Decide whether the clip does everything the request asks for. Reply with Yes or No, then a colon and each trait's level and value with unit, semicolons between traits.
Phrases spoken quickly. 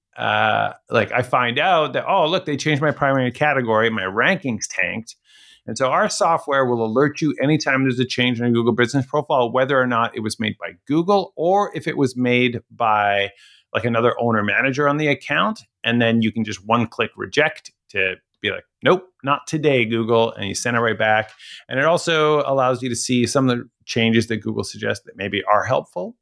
Yes: fast, 210 wpm